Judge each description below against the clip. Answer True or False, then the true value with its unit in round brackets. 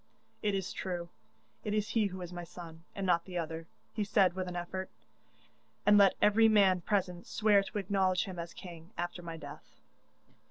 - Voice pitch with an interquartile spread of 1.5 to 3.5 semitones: True (2.6 semitones)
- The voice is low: False (185 Hz)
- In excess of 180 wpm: True (190 wpm)